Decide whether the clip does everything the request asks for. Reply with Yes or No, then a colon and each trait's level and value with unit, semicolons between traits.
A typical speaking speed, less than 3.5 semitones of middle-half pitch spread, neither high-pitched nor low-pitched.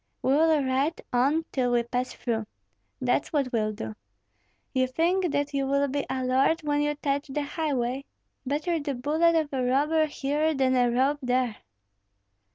No: average, 170 wpm; average, 2.8 semitones; very high, 275 Hz